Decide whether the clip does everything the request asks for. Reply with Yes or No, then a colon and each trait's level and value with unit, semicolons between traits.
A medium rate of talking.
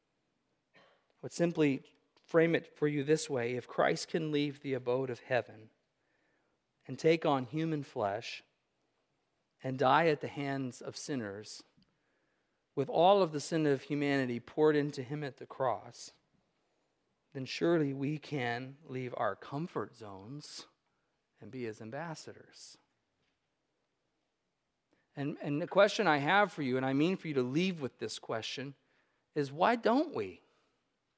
Yes: average, 145 wpm